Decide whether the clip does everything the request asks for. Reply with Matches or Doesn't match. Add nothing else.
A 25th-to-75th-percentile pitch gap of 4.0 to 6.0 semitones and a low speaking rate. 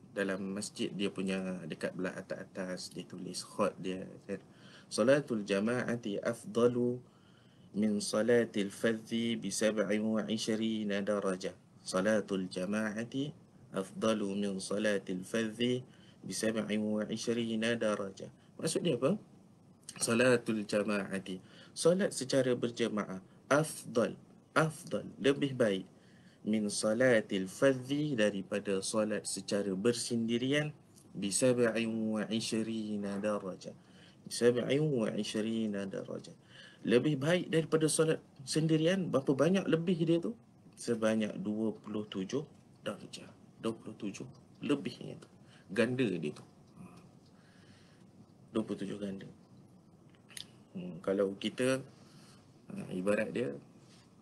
Matches